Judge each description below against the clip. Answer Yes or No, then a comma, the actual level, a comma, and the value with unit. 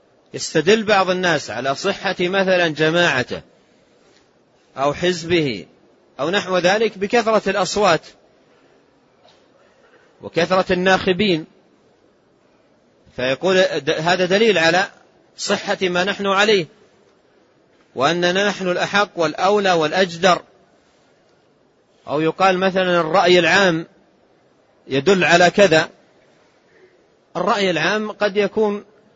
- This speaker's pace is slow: No, average, 85 wpm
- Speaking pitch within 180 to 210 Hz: Yes, medium, 185 Hz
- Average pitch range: Yes, average, 3.0 semitones